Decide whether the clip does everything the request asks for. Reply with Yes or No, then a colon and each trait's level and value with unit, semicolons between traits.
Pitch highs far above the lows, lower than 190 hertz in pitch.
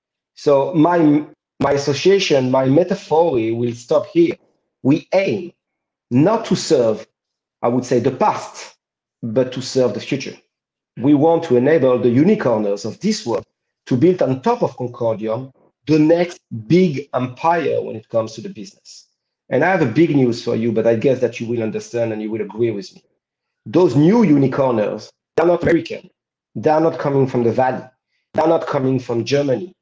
Yes: wide, 5.7 semitones; low, 135 Hz